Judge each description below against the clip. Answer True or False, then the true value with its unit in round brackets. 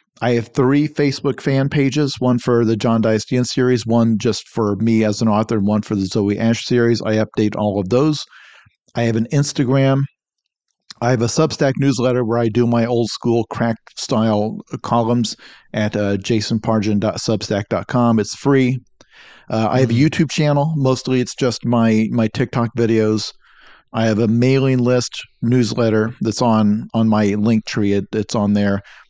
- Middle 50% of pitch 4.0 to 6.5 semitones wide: False (2.7 semitones)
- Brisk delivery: False (170 wpm)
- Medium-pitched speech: False (115 Hz)